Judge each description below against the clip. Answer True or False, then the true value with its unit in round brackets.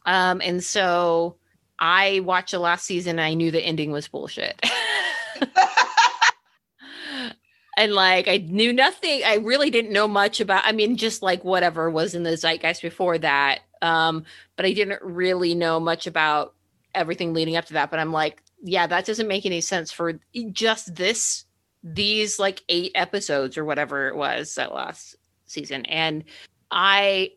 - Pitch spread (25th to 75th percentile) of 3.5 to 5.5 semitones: True (4.1 semitones)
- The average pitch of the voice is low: False (180 Hz)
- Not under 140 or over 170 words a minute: True (165 wpm)